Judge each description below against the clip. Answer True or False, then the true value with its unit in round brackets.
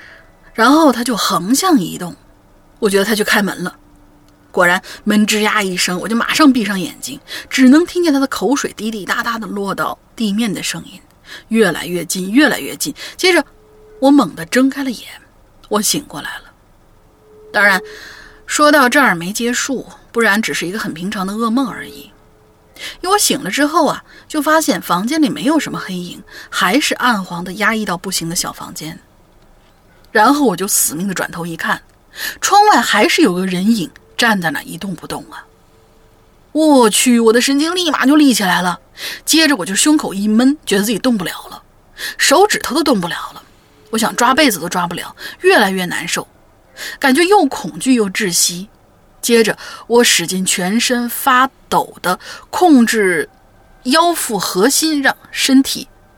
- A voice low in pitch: False (240 Hz)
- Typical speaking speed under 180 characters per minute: False (250 characters per minute)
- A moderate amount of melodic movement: False (6.8 semitones)